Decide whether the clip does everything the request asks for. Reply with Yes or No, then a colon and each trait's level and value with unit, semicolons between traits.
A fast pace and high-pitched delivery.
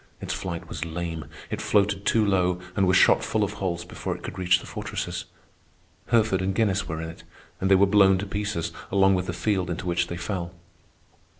No: fast, 210 wpm; very low, 95 Hz